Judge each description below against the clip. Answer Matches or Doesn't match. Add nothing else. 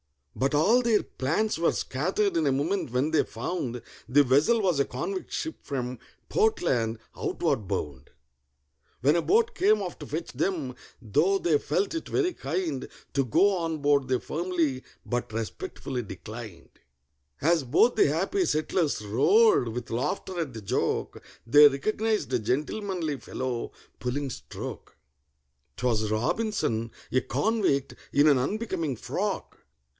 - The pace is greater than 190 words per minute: Doesn't match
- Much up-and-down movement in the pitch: Matches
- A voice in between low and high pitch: Matches